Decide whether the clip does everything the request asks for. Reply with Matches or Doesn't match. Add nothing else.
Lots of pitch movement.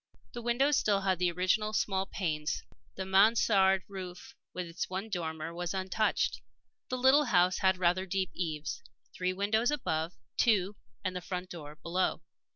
Doesn't match